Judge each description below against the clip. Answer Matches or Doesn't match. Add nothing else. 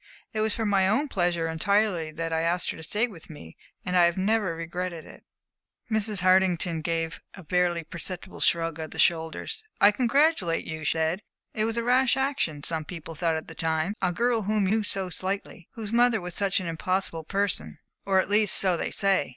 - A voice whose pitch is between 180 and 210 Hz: Matches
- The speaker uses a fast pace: Matches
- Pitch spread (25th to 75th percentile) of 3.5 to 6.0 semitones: Matches